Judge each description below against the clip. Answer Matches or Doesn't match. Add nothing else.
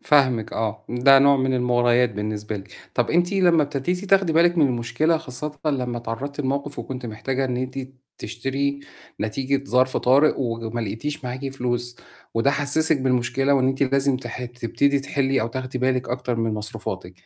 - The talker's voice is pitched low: Matches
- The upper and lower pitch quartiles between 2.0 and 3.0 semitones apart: Matches